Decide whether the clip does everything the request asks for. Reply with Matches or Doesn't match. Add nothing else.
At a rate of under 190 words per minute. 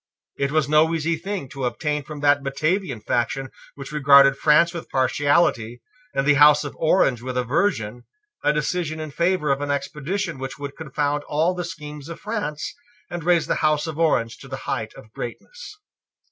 Matches